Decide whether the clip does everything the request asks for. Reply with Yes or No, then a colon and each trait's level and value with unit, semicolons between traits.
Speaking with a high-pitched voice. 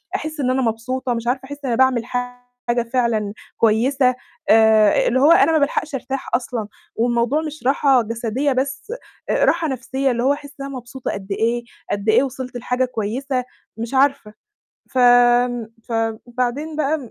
Yes: very high, 250 Hz